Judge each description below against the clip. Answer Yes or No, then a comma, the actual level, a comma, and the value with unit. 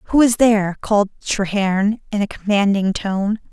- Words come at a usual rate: Yes, average, 155 wpm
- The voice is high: Yes, high, 205 Hz